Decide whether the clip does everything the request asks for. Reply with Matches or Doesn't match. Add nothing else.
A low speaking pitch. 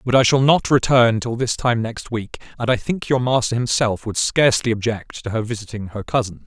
Matches